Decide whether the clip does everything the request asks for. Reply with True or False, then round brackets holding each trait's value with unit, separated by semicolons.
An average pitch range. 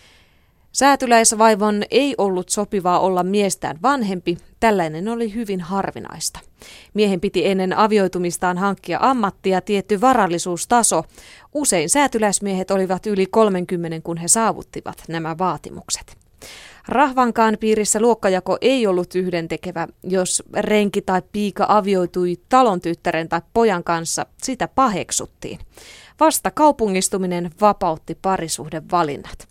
True (3.8 semitones)